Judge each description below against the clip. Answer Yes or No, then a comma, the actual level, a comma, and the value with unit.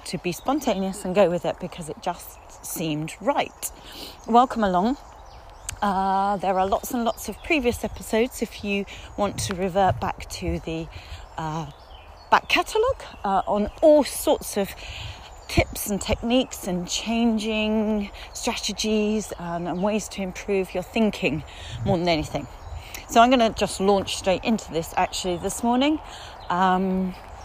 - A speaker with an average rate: Yes, average, 150 wpm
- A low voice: No, high, 200 Hz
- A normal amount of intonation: Yes, average, 3.9 semitones